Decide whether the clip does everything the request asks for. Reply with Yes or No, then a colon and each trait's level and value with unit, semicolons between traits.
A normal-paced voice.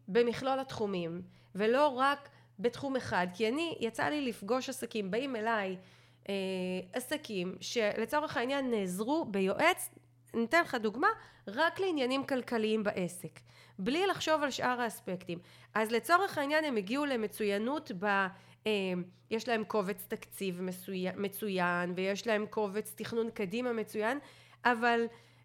Yes: average, 125 wpm